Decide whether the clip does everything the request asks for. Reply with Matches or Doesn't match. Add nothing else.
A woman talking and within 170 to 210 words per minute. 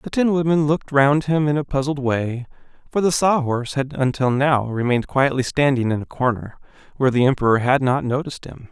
Doesn't match